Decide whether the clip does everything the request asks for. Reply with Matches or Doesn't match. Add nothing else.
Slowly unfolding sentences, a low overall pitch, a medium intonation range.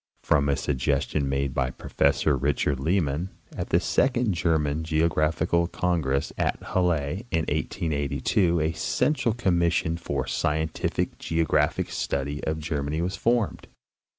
Matches